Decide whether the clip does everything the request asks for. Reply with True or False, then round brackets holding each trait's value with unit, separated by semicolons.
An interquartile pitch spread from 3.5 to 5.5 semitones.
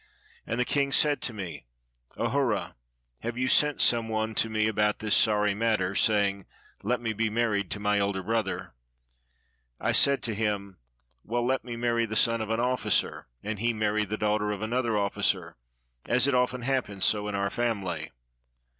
False (2.4 semitones)